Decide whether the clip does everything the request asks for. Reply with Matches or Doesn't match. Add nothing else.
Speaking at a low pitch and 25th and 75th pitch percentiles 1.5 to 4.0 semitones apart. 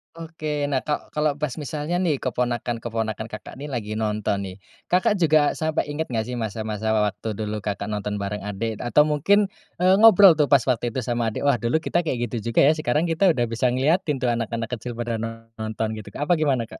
Doesn't match